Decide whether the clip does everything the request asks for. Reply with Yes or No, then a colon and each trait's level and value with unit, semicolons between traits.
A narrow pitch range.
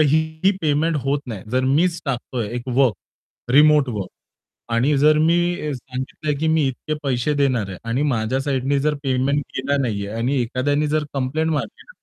No: average, 3.2 semitones